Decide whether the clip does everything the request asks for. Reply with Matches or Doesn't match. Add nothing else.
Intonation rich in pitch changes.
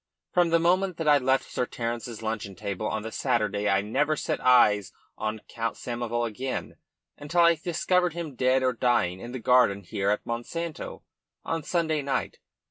Matches